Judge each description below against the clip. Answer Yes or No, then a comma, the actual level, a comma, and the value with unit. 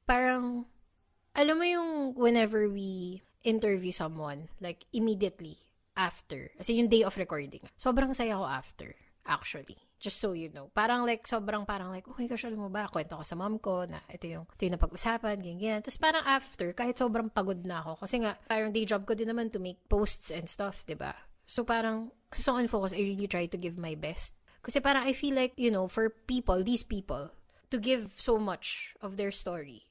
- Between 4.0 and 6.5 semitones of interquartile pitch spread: Yes, average, 4.5 semitones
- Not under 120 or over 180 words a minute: No, average, 195 wpm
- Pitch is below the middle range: No, high, 210 Hz